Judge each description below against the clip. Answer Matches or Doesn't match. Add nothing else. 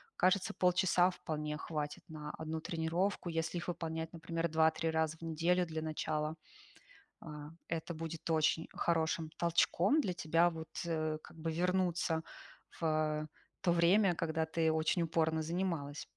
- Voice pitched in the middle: Matches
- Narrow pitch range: Matches